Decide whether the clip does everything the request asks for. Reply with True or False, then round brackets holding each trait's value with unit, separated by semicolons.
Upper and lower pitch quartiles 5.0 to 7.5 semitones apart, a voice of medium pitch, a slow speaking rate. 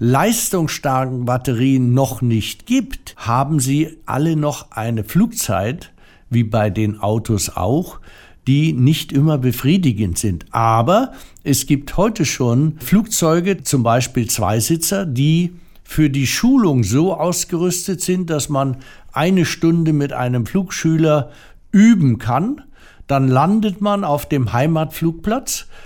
True (5.4 semitones; 145 Hz; 120 wpm)